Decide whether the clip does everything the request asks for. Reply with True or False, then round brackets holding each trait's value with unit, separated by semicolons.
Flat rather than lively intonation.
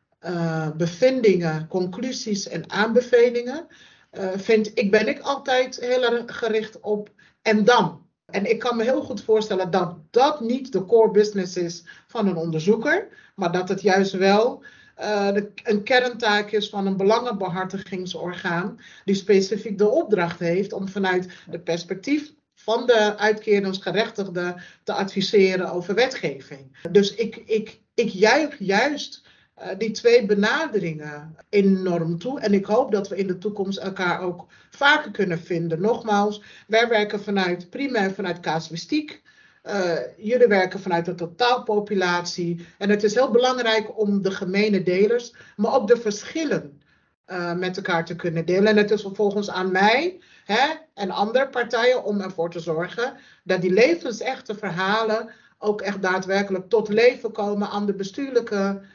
False (4.0 semitones)